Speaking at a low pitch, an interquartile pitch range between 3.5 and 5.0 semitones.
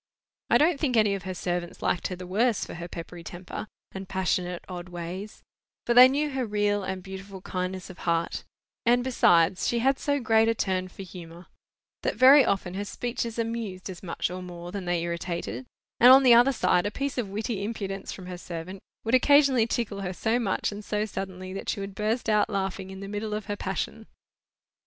No: high, 195 Hz; average, 4.0 semitones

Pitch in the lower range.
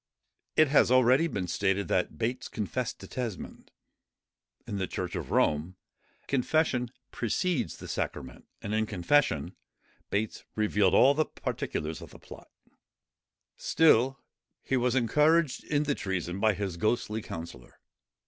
Yes: low, 110 Hz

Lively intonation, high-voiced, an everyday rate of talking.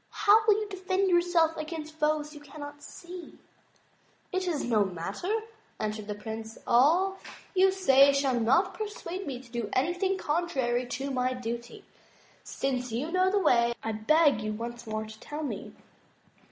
Yes: wide, 6.9 semitones; very high, 290 Hz; average, 160 wpm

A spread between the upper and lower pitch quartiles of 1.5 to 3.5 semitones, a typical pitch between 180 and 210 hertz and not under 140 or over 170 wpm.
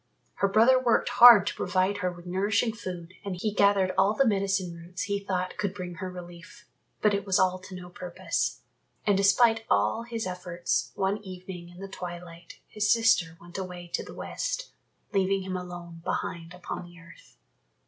No: narrow, 2.4 semitones; medium, 185 Hz; average, 180 wpm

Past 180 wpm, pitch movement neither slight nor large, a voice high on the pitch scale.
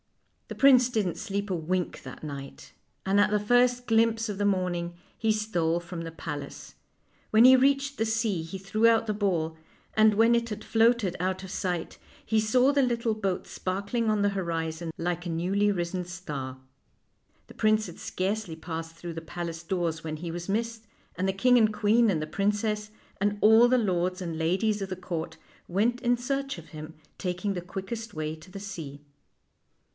Yes: average, 190 wpm; average, 4.5 semitones; high, 195 Hz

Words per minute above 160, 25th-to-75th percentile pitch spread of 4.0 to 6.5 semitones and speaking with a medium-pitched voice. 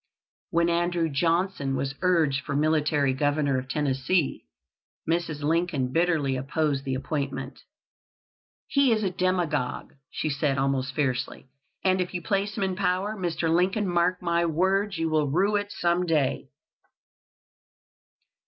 No: slow, 135 wpm; average, 4.6 semitones; medium, 165 Hz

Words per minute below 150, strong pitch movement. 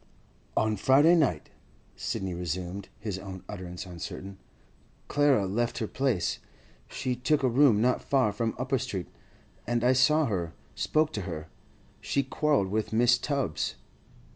Yes: average, 140 wpm; wide, 5.9 semitones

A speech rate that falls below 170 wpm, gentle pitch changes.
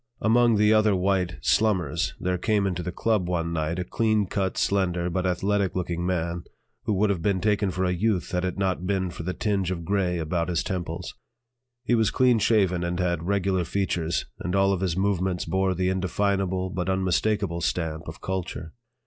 No: average, 190 wpm; narrow, 2.2 semitones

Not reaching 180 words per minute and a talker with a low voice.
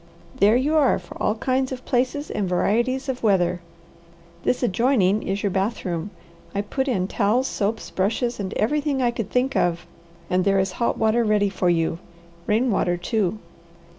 No: average, 170 wpm; high, 215 Hz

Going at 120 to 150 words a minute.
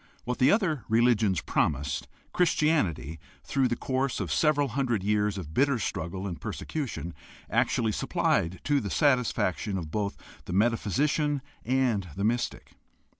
Yes: slow, 135 wpm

